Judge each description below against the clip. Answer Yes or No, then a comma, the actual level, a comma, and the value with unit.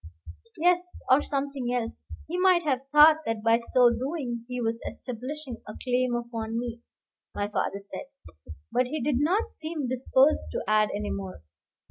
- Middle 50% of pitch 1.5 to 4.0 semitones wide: No, average, 4.5 semitones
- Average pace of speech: Yes, average, 160 wpm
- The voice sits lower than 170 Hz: No, very high, 250 Hz